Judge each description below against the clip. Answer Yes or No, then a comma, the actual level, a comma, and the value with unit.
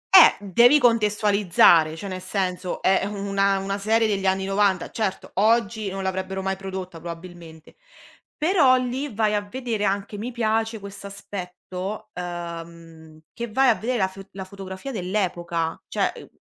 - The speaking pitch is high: Yes, high, 195 Hz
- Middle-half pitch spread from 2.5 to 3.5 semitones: Yes, average, 2.8 semitones